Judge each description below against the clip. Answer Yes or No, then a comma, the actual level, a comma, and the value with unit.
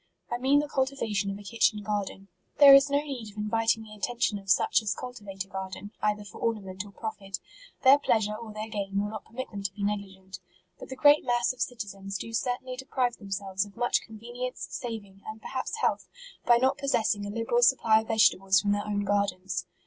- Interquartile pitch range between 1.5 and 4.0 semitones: Yes, average, 3.4 semitones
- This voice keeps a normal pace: No, fast, 210 wpm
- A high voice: Yes, high, 215 Hz